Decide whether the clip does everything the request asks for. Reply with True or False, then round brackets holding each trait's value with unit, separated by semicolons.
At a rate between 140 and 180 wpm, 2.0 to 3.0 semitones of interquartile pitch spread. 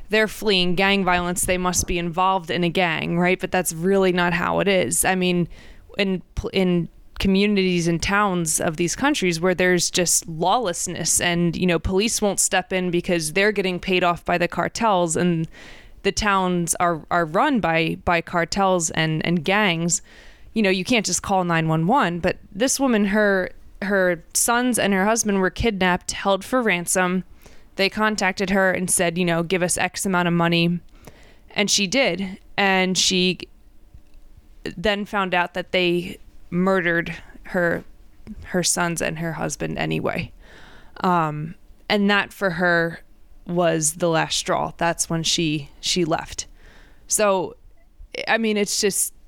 True (160 wpm; 2.4 semitones)